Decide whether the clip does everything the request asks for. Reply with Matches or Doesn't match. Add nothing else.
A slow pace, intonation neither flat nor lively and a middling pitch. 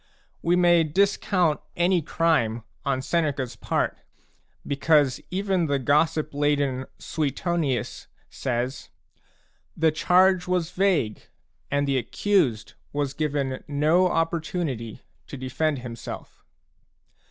Matches